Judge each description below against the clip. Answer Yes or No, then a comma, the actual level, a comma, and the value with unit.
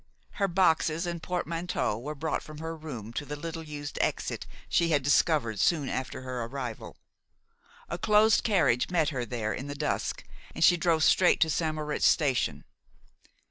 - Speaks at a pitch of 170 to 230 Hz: No, medium, 155 Hz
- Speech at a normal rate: Yes, average, 170 wpm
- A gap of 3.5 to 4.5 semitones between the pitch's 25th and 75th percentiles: Yes, average, 4.0 semitones